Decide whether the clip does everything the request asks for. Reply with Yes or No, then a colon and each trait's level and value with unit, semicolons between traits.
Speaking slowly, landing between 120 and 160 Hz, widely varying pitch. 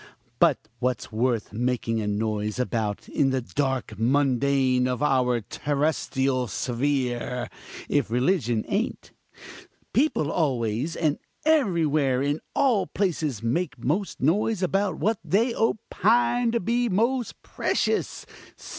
Yes: slow, 115 wpm; medium, 140 Hz; wide, 7.7 semitones